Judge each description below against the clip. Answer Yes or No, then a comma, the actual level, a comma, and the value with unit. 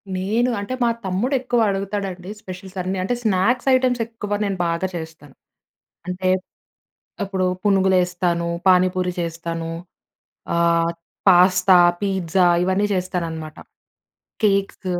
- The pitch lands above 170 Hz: Yes, medium, 185 Hz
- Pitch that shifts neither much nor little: No, narrow, 2.1 semitones